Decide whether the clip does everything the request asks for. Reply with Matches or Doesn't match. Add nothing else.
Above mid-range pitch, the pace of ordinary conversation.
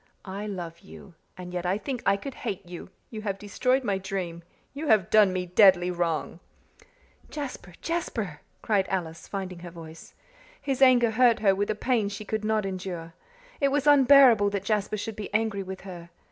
Matches